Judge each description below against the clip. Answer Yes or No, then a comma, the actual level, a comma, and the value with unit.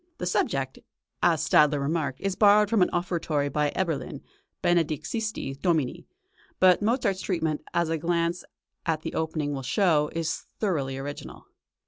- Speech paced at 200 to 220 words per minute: No, average, 140 wpm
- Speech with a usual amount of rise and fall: Yes, average, 3.8 semitones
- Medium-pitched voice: Yes, medium, 165 Hz